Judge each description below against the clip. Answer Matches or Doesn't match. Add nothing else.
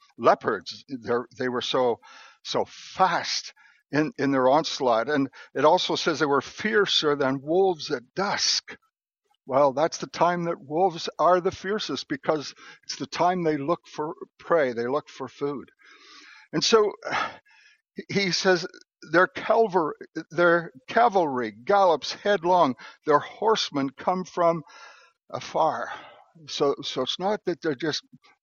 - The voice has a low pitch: Doesn't match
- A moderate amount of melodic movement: Doesn't match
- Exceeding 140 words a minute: Doesn't match